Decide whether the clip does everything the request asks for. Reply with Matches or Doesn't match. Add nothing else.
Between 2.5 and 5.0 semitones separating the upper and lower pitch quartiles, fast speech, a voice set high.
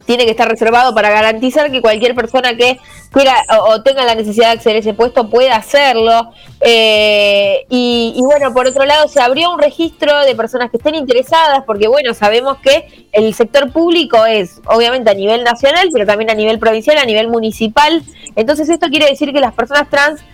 Matches